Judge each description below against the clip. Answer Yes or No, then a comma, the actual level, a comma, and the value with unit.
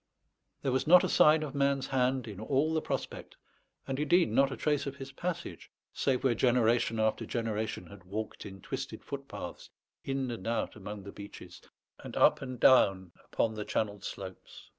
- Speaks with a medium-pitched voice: No, low, 125 Hz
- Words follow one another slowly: No, average, 180 wpm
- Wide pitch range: No, average, 4.6 semitones